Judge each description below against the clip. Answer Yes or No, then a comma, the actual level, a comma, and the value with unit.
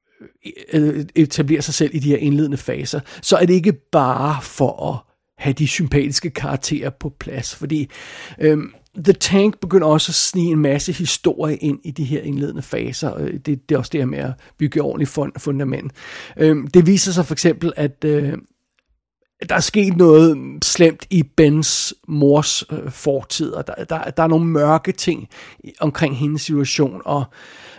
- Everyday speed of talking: Yes, average, 175 wpm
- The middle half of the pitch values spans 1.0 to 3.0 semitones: Yes, narrow, 2.6 semitones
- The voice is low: No, medium, 150 Hz